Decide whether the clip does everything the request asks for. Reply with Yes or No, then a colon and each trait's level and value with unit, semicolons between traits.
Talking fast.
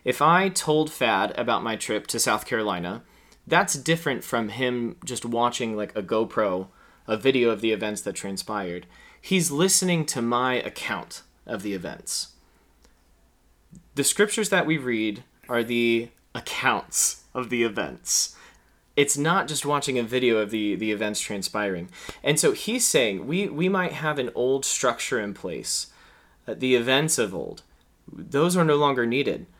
No: average, 160 wpm